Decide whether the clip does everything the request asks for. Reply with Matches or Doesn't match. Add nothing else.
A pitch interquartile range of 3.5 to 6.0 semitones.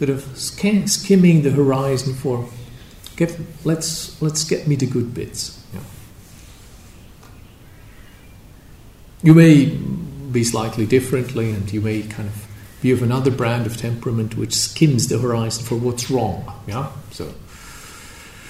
Matches